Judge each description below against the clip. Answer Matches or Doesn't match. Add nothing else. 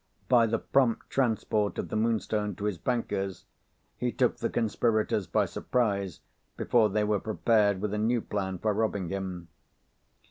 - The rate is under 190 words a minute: Matches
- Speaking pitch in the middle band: Doesn't match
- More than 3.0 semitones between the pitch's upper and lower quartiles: Doesn't match